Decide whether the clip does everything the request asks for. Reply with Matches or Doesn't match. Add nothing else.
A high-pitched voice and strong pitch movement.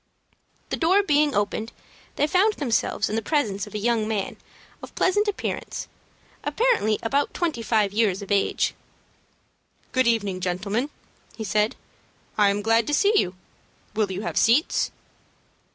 Matches